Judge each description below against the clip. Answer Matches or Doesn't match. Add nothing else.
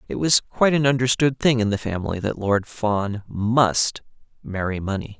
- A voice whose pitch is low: Matches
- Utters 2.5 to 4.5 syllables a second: Doesn't match